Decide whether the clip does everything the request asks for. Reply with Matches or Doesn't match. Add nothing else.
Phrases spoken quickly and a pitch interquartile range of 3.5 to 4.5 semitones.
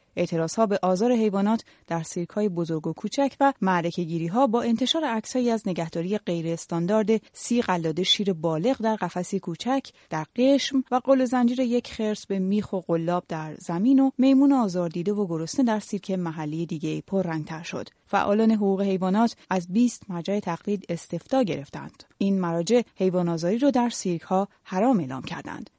Doesn't match